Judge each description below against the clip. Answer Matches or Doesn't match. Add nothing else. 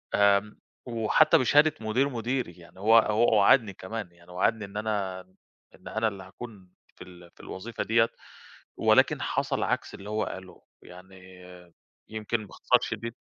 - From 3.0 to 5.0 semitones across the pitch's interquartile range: Matches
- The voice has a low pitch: Matches